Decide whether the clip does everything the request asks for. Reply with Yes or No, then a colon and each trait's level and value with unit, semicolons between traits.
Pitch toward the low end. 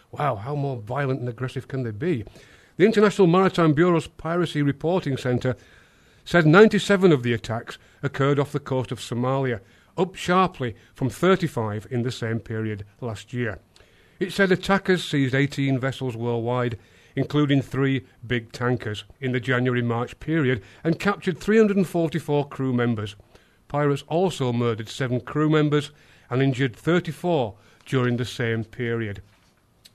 Yes: low, 130 Hz